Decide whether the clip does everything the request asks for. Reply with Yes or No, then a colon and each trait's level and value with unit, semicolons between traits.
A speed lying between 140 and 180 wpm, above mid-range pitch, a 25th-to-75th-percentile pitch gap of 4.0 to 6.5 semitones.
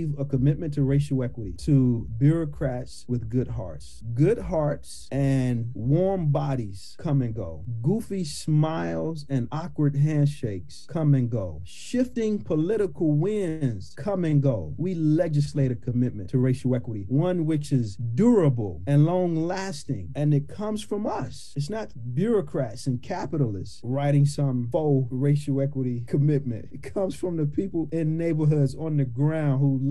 No: average, 150 wpm; medium, 140 Hz; average, 4.3 semitones